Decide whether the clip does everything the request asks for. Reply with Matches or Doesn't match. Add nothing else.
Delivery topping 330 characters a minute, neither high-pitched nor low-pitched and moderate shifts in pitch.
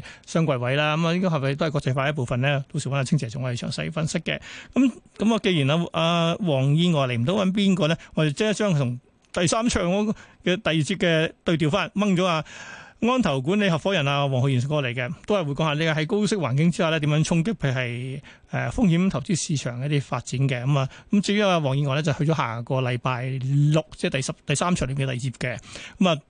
Matches